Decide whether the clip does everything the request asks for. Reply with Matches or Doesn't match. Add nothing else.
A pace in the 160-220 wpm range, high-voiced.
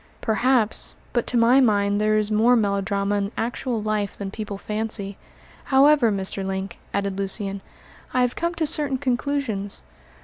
Doesn't match